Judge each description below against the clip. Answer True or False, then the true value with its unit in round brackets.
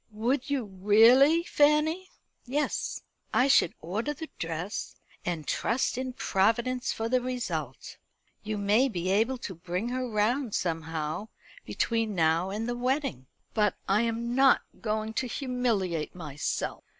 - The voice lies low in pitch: False (225 Hz)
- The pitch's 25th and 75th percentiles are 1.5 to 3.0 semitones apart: False (5.3 semitones)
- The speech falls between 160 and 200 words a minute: False (140 wpm)